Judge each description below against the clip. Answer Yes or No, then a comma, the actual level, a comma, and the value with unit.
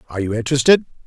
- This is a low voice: Yes, low, 130 Hz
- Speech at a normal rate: Yes, average, 170 wpm